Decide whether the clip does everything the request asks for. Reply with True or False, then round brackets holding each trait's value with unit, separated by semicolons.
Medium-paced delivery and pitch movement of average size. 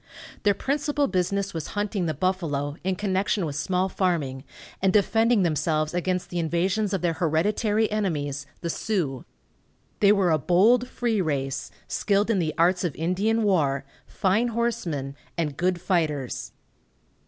True (145 wpm; 4.6 semitones)